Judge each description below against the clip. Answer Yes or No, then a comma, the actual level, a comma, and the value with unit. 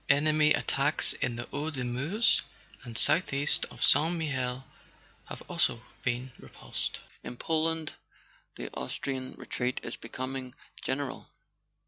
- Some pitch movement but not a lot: Yes, average, 3.3 semitones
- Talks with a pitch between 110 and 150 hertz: Yes, medium, 140 Hz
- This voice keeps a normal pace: No, slow, 125 wpm